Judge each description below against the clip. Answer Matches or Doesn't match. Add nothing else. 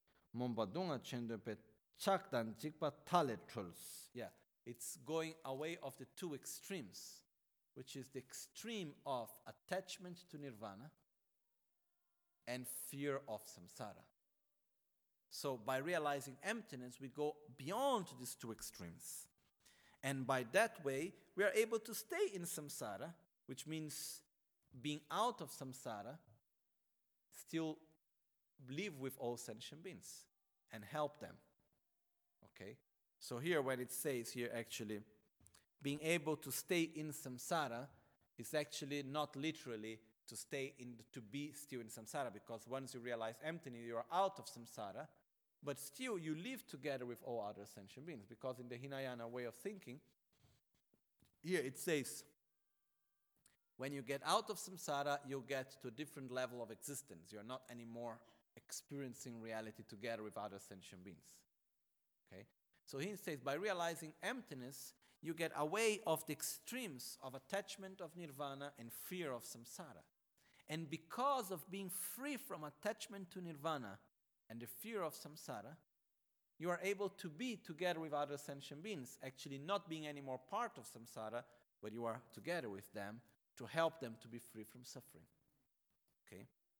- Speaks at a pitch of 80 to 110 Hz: Doesn't match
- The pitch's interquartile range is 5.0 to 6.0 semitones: Matches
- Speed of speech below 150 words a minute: Matches